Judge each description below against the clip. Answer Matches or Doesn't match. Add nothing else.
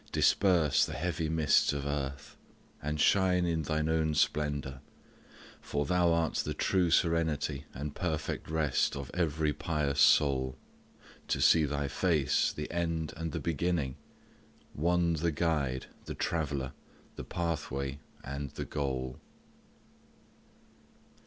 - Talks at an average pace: Doesn't match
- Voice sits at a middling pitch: Doesn't match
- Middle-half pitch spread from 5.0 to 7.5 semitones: Doesn't match